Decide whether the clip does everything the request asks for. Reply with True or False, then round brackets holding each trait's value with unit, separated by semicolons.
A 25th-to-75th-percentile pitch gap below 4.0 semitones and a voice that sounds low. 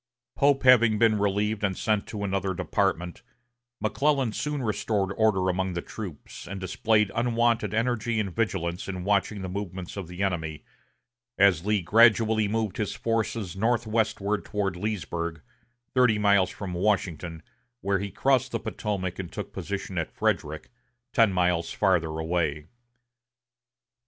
True (3.4 semitones; 100 Hz)